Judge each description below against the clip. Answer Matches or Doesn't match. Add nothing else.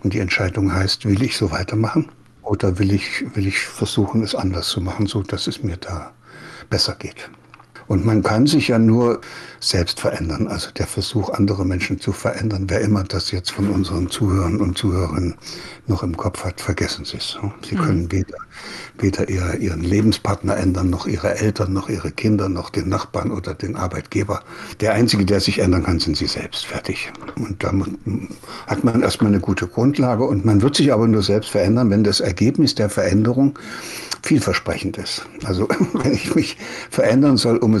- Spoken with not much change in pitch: Matches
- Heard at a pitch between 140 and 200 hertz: Doesn't match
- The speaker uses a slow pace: Doesn't match